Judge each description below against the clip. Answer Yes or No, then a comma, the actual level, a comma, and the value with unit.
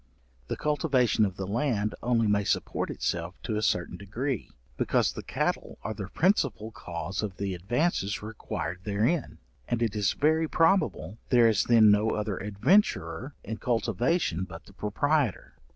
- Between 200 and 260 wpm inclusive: No, average, 155 wpm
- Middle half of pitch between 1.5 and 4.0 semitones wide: No, average, 4.6 semitones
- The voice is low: Yes, low, 110 Hz